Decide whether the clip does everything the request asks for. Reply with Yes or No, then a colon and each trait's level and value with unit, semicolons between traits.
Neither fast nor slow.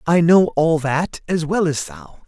No: fast, 210 wpm